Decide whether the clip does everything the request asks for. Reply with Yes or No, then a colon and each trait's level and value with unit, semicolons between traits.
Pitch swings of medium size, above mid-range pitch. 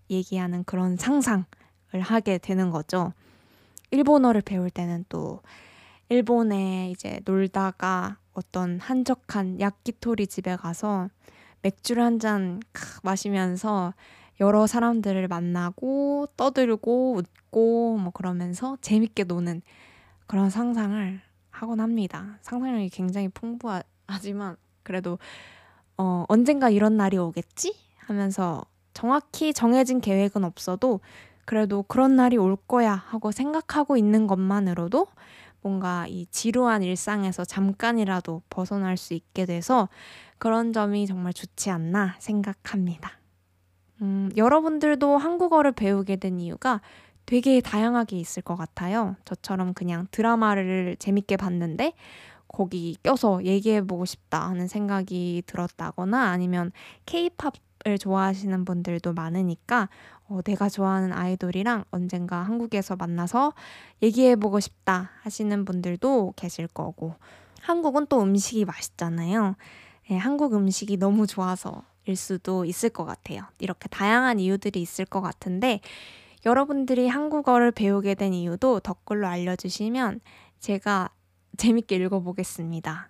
Yes: average, 3.9 semitones; high, 195 Hz